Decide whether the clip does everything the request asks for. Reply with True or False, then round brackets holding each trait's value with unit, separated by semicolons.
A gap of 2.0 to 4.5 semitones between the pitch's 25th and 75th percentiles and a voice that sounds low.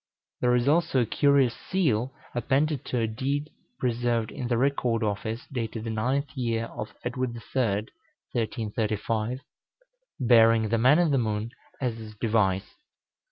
True (2.8 semitones; 120 Hz)